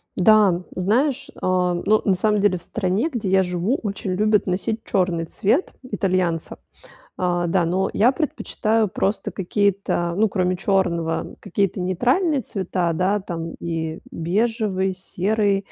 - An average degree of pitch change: Yes, average, 3.2 semitones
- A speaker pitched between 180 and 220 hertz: Yes, high, 190 Hz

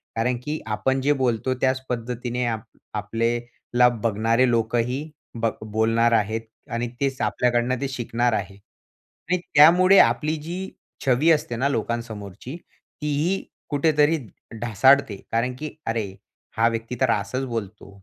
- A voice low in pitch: Yes, low, 120 Hz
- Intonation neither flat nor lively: Yes, average, 3.1 semitones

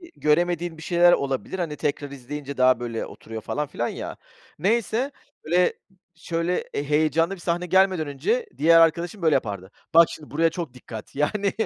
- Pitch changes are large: No, average, 3.8 semitones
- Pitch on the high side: No, medium, 160 Hz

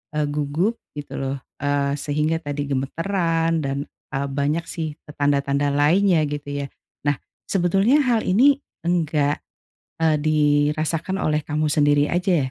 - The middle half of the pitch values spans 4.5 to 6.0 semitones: No, average, 2.7 semitones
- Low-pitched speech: No, medium, 150 Hz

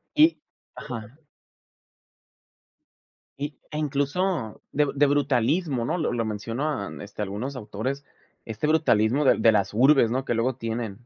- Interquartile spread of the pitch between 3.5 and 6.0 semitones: Yes, average, 4.8 semitones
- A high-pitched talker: No, low, 130 Hz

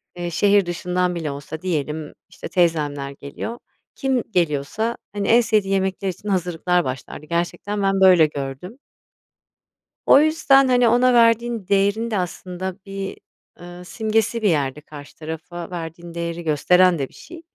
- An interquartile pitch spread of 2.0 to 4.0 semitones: No, average, 4.4 semitones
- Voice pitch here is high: No, medium, 180 Hz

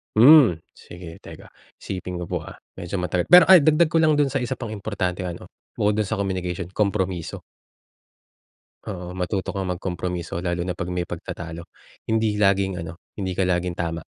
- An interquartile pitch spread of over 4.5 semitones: No, average, 3.7 semitones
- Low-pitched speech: Yes, very low, 95 Hz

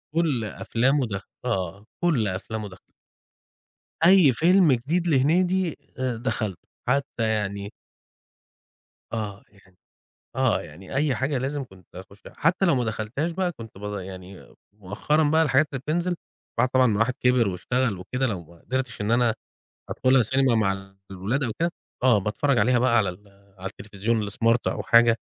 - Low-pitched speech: Yes, low, 115 Hz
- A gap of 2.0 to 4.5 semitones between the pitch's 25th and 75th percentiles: No, average, 5.3 semitones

